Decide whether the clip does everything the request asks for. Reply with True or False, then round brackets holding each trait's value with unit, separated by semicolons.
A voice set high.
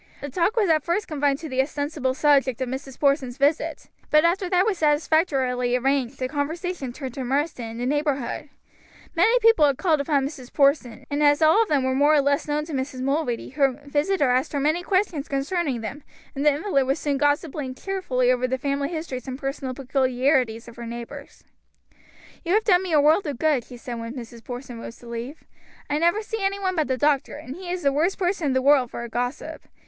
True (285 Hz)